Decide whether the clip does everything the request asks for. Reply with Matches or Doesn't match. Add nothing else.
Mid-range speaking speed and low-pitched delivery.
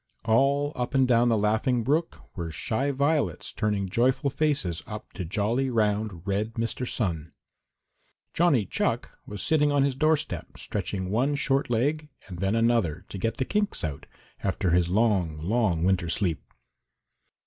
Matches